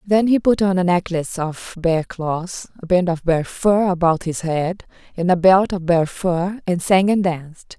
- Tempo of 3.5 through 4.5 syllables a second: Yes, 4.3 syllables/s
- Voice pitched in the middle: Yes, medium, 180 Hz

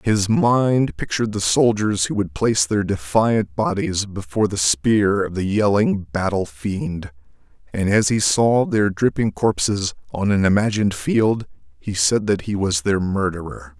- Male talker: Yes, male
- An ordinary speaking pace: Yes, average, 160 wpm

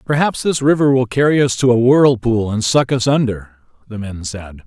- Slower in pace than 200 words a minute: No, fast, 205 wpm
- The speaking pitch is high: No, low, 120 Hz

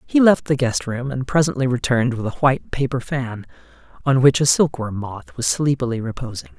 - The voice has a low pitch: Yes, low, 125 Hz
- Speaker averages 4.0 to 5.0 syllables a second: No, 5.4 syllables/s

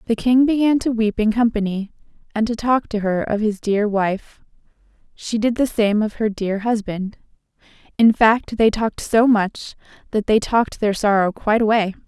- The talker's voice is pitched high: Yes, high, 220 Hz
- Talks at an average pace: Yes, average, 180 wpm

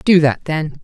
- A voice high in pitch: No, medium, 155 Hz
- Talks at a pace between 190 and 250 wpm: Yes, fast, 215 wpm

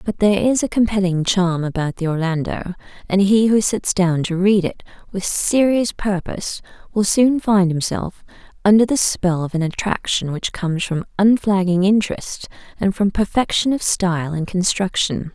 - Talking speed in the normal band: Yes, average, 165 wpm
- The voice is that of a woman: Yes, female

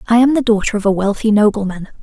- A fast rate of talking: Yes, fast, 235 wpm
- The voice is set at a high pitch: Yes, high, 215 Hz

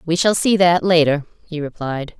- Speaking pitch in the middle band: Yes, medium, 165 Hz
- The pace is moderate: Yes, average, 190 wpm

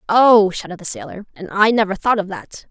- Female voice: Yes, female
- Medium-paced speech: No, fast, 220 wpm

